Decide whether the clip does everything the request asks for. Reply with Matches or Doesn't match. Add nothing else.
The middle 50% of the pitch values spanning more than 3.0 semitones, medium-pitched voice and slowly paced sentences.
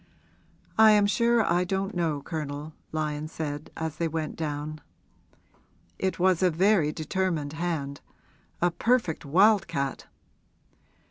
Matches